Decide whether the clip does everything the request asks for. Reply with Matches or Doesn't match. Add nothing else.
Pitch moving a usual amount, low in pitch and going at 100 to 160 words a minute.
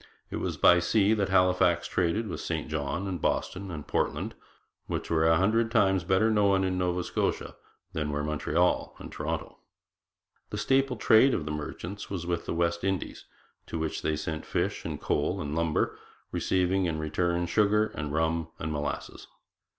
Doesn't match